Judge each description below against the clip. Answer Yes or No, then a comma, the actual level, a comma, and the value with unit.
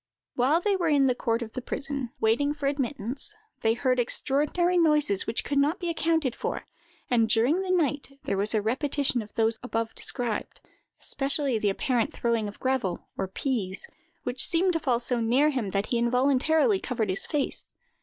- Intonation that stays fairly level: No, average, 4.4 semitones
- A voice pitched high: Yes, very high, 255 Hz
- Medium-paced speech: Yes, average, 180 wpm